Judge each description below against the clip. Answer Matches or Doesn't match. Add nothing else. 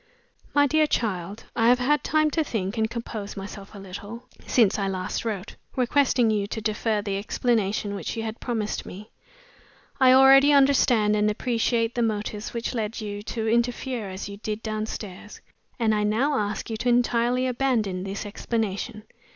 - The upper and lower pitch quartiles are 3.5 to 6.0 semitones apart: Doesn't match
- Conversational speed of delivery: Matches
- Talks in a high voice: Matches